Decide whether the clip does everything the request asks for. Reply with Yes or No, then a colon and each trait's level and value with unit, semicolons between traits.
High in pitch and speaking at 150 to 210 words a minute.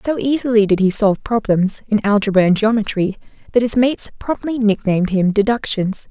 Yes: high, 215 Hz; average, 165 wpm